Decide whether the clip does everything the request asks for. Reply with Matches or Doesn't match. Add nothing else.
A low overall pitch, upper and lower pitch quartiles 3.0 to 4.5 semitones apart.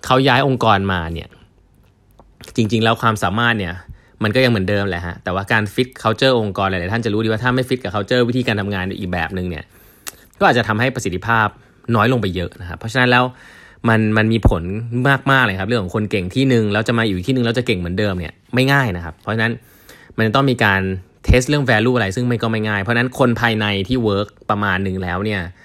Matches